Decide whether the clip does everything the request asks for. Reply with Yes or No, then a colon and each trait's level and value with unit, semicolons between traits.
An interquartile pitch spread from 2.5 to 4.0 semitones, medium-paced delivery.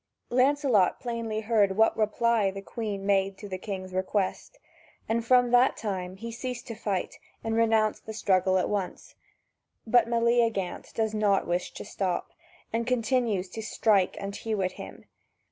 Yes: average, 3.1 semitones; average, 160 wpm